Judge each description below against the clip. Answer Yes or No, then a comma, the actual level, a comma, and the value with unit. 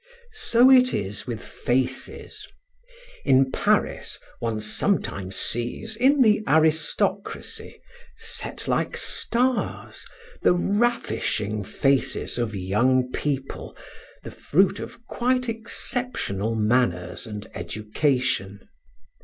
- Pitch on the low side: Yes, low, 130 Hz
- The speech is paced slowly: Yes, slow, 95 wpm